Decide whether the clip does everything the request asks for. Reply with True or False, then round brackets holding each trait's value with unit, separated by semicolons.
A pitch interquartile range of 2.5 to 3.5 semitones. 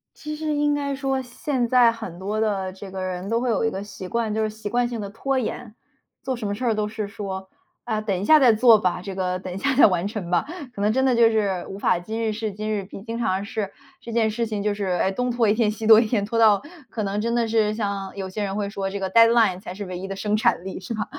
True (2.9 semitones)